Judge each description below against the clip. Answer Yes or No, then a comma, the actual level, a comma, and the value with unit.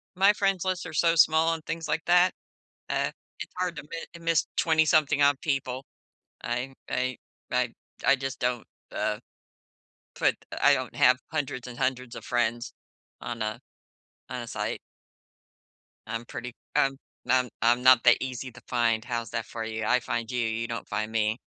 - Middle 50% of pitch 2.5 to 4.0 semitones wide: No, average, 4.7 semitones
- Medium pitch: No, low, 125 Hz